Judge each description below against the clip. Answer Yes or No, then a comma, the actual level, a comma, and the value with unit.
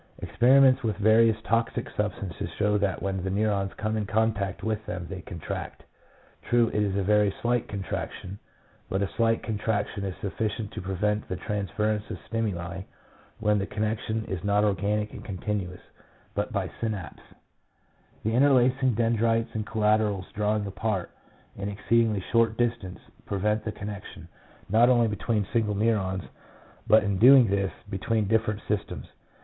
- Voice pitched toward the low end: Yes, low, 105 Hz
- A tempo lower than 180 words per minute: Yes, average, 150 wpm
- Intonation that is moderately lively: No, narrow, 2.2 semitones